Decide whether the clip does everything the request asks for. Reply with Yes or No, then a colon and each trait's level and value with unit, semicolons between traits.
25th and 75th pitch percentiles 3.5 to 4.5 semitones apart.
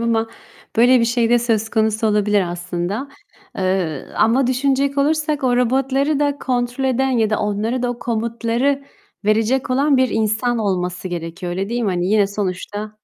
Yes: average, 3.9 semitones